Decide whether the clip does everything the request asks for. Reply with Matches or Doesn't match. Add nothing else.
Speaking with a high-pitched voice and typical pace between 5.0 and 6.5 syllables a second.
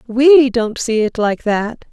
Doesn't match